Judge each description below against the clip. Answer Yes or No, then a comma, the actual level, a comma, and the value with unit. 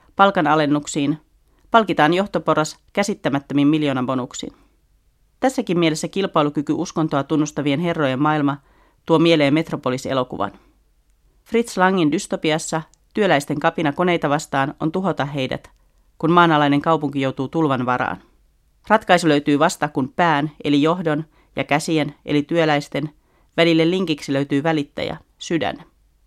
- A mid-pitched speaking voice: Yes, medium, 155 Hz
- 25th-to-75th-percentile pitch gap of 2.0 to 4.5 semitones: Yes, average, 2.7 semitones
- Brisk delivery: No, average, 110 wpm